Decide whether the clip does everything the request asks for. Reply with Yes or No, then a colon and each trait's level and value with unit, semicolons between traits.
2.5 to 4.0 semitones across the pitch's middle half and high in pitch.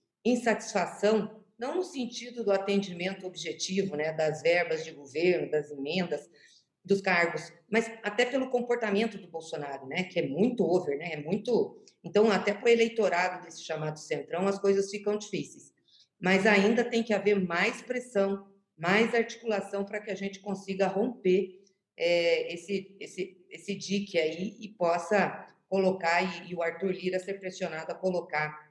Yes: average, 3.6 semitones; high, 195 Hz